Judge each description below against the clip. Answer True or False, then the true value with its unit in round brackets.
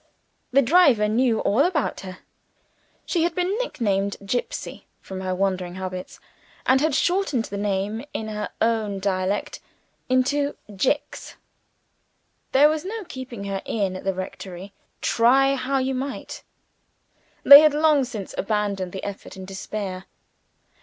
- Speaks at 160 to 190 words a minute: False (140 wpm)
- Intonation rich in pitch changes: True (6.1 semitones)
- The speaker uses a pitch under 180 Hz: False (220 Hz)